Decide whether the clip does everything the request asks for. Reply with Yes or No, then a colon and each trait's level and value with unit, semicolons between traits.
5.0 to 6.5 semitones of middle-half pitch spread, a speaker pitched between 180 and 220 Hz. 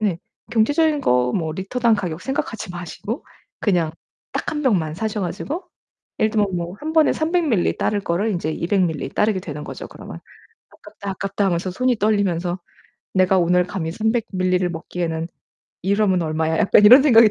No: average, 4.5 semitones; high, 190 Hz